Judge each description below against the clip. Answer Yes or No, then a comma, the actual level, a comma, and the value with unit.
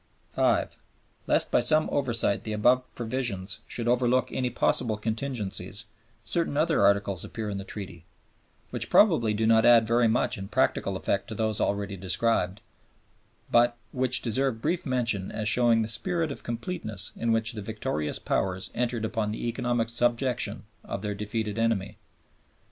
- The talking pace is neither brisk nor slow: Yes, average, 155 wpm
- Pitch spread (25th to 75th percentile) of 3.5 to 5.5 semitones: No, average, 2.8 semitones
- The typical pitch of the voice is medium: No, low, 115 Hz